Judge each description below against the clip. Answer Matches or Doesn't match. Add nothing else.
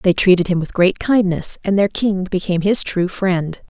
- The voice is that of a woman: Matches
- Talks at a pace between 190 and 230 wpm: Matches